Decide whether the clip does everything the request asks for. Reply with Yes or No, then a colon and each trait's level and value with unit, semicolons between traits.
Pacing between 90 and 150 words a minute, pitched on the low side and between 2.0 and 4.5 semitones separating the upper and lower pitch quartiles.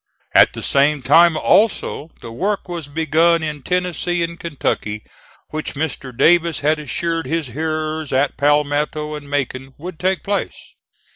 No: average, 145 wpm; medium, 155 Hz; average, 2.8 semitones